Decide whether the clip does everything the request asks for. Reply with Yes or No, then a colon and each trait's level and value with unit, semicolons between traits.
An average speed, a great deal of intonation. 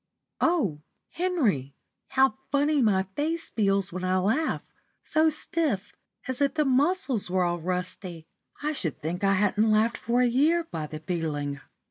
Yes: average, 155 wpm; wide, 8.3 semitones